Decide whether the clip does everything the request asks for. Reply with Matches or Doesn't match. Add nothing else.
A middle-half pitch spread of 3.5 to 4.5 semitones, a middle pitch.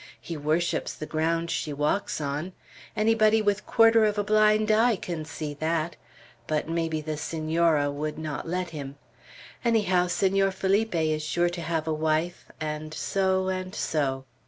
Matches